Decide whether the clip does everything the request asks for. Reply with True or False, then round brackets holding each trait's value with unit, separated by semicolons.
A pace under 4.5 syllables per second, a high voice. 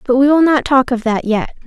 False (5.4 syllables/s; 260 Hz)